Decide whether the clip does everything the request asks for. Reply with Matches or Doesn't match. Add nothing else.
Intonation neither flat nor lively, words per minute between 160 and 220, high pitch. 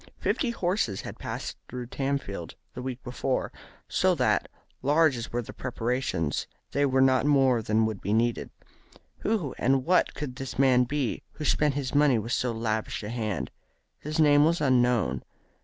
Doesn't match